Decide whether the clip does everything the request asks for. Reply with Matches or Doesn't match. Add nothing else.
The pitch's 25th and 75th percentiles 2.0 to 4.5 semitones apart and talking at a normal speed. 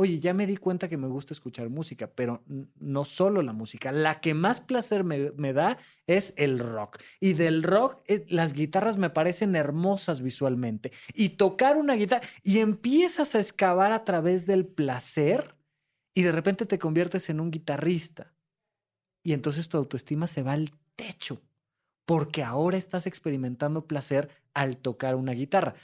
Doesn't match